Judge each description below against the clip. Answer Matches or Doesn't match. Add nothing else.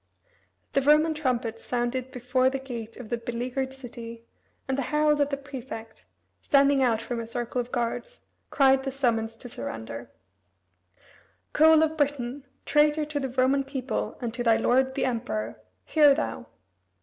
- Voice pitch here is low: Doesn't match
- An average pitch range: Matches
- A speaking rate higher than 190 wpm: Doesn't match